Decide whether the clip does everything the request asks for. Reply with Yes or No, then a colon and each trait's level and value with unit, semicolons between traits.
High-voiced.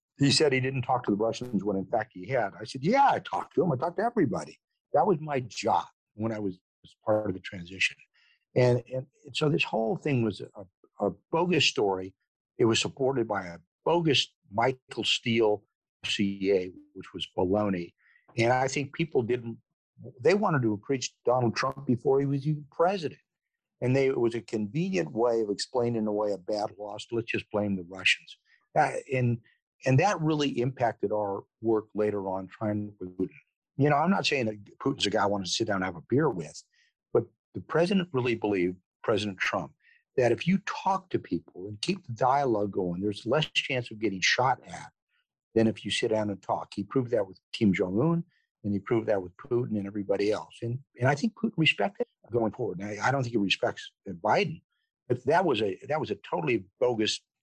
No: low, 115 Hz